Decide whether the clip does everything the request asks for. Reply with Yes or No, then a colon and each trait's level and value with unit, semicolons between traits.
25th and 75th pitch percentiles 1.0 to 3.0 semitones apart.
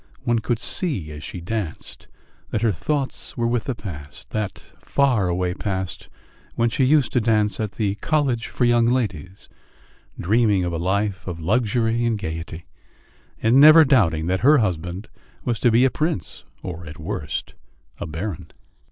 No: average, 5.2 semitones